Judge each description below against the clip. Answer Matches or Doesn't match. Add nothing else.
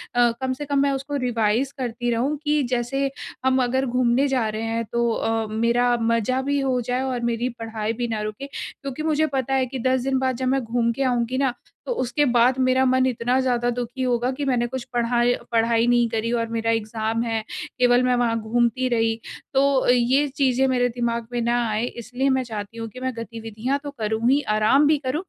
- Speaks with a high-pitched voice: Matches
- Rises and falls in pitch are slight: Matches